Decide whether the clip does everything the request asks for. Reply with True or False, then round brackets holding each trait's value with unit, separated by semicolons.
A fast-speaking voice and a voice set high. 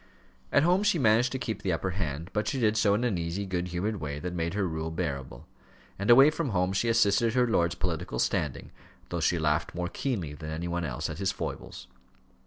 False (220 wpm; 90 Hz)